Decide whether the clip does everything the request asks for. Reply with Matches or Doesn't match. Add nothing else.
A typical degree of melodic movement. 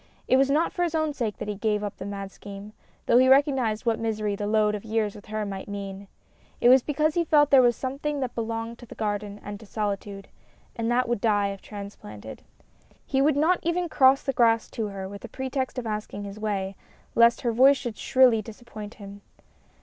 Matches